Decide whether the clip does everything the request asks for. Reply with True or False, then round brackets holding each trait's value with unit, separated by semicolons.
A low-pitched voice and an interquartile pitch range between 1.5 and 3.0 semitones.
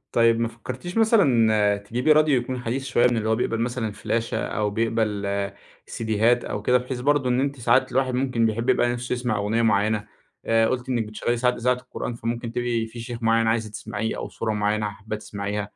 True (115 Hz; 2.4 semitones)